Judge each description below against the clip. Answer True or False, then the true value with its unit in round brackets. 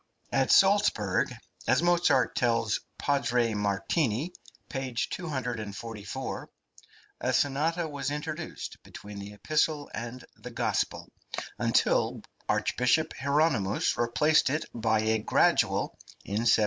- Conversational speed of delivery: False (105 wpm)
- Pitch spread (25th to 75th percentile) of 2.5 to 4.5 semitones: False (5.5 semitones)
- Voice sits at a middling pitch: False (125 Hz)